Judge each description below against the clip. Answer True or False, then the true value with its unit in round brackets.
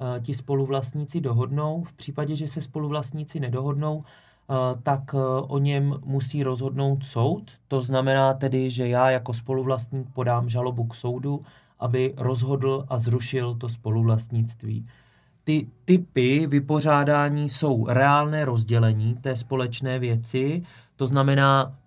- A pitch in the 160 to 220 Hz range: False (135 Hz)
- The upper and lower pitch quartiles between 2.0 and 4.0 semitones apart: True (2.3 semitones)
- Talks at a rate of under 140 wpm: True (120 wpm)